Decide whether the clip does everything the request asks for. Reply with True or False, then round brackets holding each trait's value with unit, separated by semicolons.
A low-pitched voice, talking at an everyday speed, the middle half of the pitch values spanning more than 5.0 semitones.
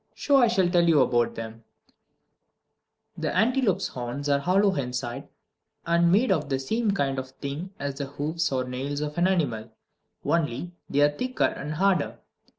False (150 Hz; 170 wpm; 5.6 semitones)